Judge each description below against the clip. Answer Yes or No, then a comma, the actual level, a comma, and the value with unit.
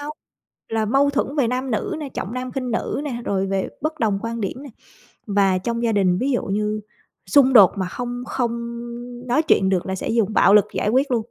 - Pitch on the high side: Yes, high, 235 Hz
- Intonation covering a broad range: No, average, 4.3 semitones